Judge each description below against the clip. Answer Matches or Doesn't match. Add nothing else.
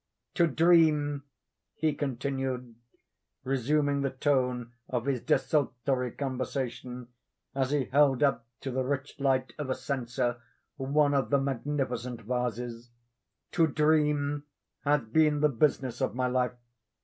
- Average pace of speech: Doesn't match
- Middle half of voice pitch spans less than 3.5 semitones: Matches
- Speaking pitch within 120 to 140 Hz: Matches